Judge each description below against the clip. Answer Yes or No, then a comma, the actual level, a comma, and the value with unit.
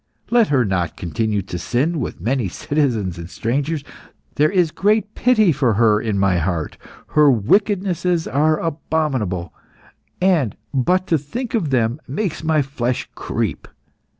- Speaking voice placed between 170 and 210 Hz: No, medium, 140 Hz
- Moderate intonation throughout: No, wide, 7.6 semitones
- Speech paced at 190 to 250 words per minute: No, average, 145 wpm